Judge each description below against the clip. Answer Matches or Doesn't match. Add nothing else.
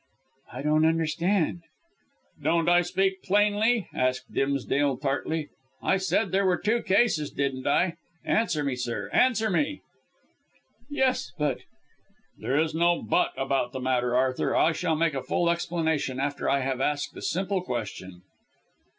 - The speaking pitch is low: Doesn't match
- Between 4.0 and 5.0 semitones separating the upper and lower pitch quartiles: Doesn't match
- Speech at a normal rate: Matches